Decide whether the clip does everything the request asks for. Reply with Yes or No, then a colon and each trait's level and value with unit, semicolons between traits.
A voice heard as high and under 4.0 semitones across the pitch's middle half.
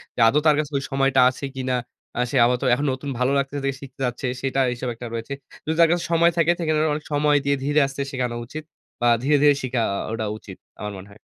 No: low, 135 Hz; average, 3.0 semitones